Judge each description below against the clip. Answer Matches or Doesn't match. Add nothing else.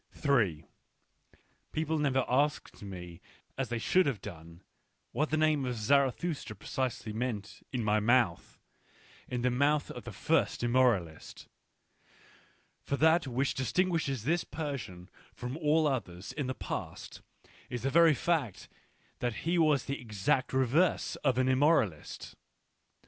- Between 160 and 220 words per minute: Doesn't match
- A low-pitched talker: Matches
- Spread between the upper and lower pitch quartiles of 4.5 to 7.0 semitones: Matches